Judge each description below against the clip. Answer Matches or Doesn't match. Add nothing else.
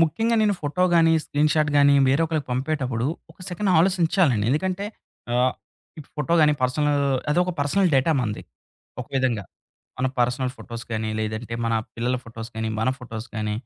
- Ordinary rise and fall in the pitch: Doesn't match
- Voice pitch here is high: Doesn't match